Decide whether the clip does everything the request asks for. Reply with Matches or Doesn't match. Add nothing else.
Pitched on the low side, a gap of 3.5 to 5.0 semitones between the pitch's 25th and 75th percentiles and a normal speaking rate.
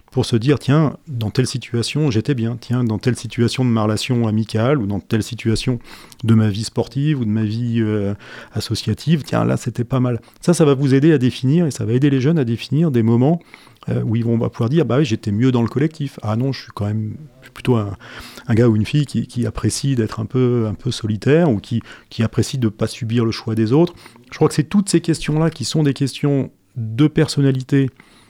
Doesn't match